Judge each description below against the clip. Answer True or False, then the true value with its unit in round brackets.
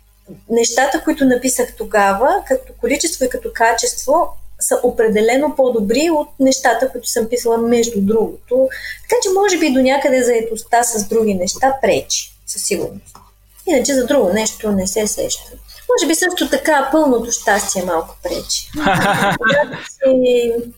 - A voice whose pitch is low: False (250 Hz)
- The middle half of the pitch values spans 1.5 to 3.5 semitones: False (4.5 semitones)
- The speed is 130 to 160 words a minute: True (135 wpm)